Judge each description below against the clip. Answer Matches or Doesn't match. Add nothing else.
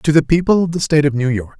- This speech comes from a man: Matches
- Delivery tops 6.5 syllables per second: Matches